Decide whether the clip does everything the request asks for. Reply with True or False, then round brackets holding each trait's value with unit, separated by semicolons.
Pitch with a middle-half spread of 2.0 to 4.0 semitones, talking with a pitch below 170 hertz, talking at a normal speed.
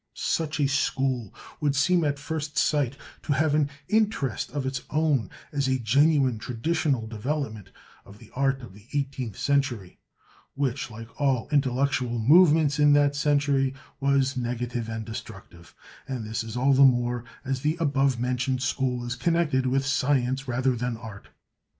True (2.9 semitones; 135 Hz; 155 wpm)